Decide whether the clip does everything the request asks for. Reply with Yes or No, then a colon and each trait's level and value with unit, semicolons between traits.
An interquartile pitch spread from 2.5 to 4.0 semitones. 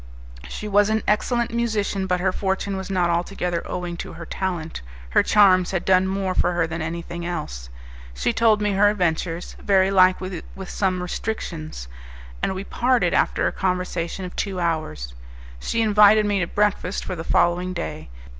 Yes: average, 2.8 semitones